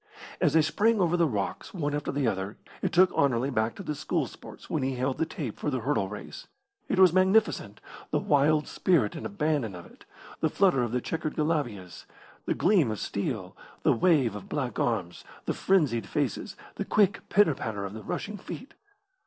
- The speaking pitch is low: No, medium, 145 Hz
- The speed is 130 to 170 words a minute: No, average, 195 wpm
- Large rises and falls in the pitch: Yes, wide, 7.4 semitones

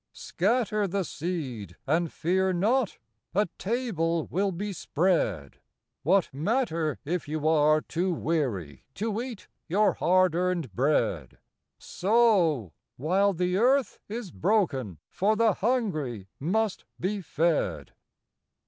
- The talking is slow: Yes, slow, 120 wpm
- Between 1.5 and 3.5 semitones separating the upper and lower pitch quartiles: No, average, 5.2 semitones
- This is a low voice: No, medium, 180 Hz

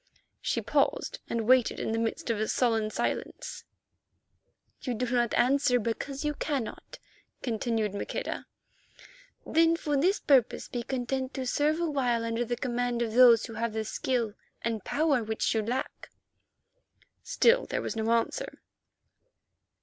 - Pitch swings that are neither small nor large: Yes, average, 3.1 semitones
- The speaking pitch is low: No, high, 240 Hz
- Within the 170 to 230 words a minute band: No, average, 145 wpm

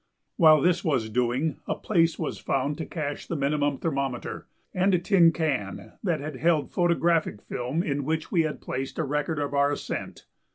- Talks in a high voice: No, medium, 150 Hz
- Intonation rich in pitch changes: No, average, 3.2 semitones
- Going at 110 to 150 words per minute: No, average, 190 wpm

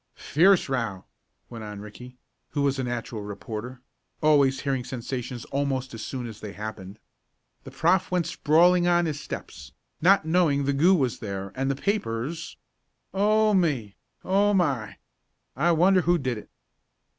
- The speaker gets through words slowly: No, average, 155 wpm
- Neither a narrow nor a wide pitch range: No, wide, 7.0 semitones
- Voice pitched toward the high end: No, low, 135 Hz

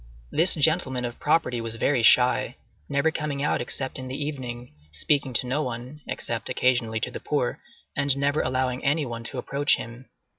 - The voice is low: Yes, low, 130 Hz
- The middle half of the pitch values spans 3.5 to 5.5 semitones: No, average, 2.9 semitones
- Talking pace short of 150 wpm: No, average, 175 wpm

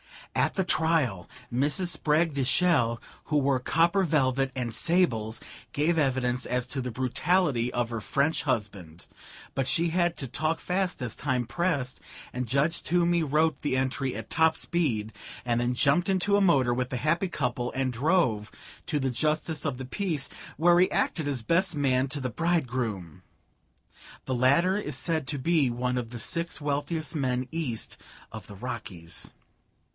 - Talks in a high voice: No, medium, 140 Hz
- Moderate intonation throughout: Yes, average, 4.9 semitones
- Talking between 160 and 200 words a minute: Yes, average, 170 wpm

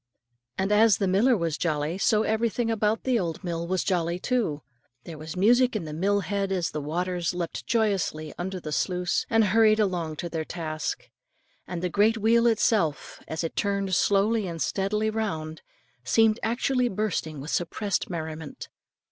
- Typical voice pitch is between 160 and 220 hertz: Yes, high, 190 Hz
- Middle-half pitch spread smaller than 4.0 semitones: No, average, 4.7 semitones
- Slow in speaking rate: No, average, 175 wpm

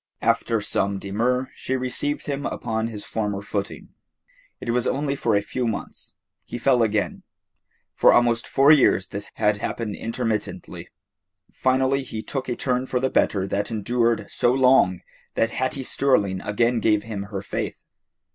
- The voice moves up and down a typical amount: Yes, average, 3.7 semitones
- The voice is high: No, low, 115 Hz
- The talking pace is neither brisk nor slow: Yes, average, 155 wpm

